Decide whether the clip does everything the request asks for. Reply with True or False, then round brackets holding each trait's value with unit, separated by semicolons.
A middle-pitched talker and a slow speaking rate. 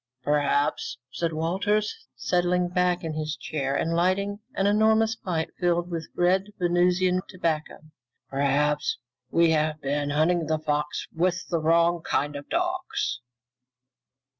True (170 Hz; 130 wpm)